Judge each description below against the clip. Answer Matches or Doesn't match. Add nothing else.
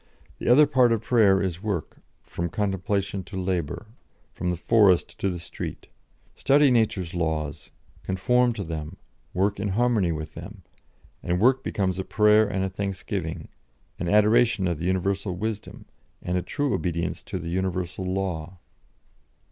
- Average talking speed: Matches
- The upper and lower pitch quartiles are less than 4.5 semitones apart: Matches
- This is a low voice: Matches